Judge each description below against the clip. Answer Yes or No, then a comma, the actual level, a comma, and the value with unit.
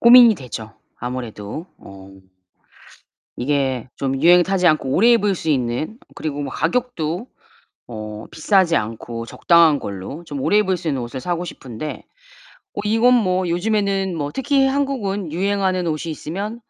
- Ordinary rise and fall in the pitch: No, wide, 7.2 semitones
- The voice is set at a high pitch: No, medium, 170 Hz